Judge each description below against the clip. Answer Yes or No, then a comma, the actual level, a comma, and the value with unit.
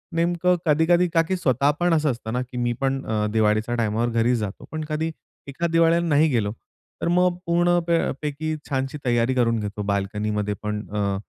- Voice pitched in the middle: No, low, 130 Hz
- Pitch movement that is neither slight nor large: No, wide, 6.8 semitones